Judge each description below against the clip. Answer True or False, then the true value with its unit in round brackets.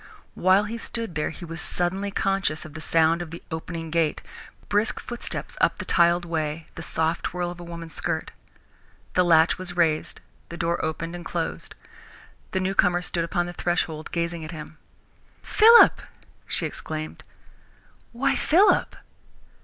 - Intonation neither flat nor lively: False (2.3 semitones)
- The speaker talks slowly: False (155 wpm)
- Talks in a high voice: False (170 Hz)